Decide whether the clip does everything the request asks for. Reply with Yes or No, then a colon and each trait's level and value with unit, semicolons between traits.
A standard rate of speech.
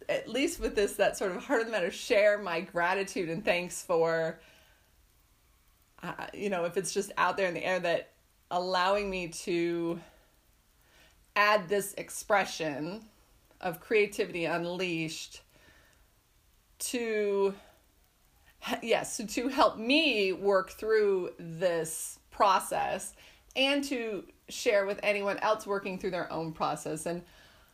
No: slow, 130 wpm